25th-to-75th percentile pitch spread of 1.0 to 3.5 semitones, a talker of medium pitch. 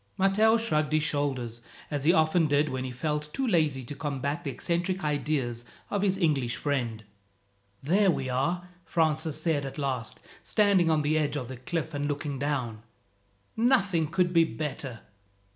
No: average, 4.0 semitones; medium, 150 Hz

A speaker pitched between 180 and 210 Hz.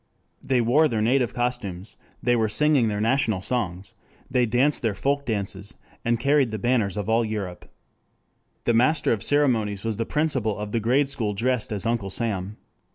No: low, 115 Hz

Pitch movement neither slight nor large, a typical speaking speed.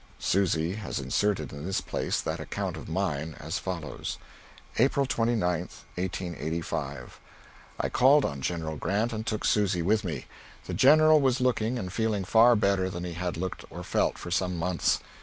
Yes: average, 4.7 semitones; average, 165 wpm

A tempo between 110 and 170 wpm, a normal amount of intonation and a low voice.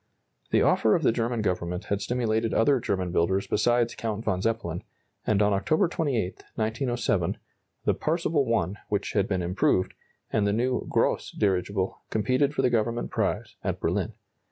Yes: average, 160 wpm; average, 3.8 semitones; low, 110 Hz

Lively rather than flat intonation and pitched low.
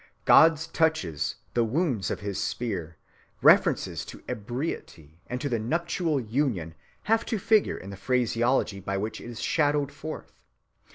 Yes: wide, 7.6 semitones; low, 125 Hz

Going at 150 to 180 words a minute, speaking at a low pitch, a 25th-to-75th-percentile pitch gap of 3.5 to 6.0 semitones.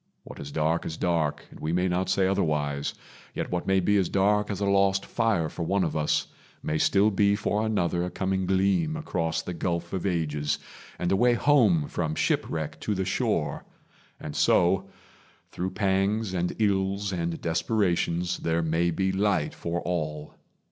No: average, 175 wpm; very low, 90 Hz; average, 3.1 semitones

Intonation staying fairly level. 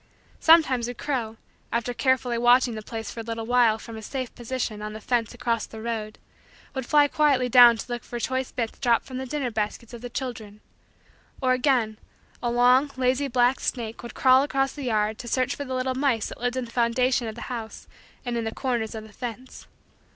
Yes: narrow, 2.3 semitones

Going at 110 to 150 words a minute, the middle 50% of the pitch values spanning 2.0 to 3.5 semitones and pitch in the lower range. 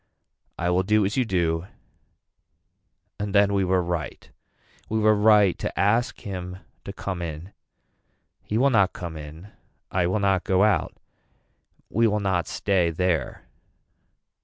Yes: average, 145 wpm; average, 2.8 semitones; very low, 95 Hz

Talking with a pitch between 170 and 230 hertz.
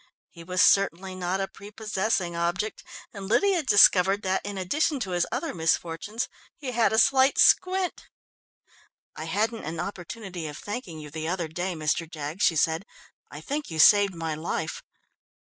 Yes: high, 190 Hz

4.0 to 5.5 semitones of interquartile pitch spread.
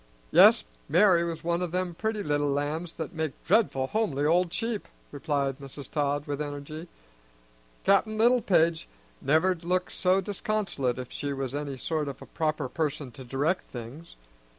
Yes: average, 4.3 semitones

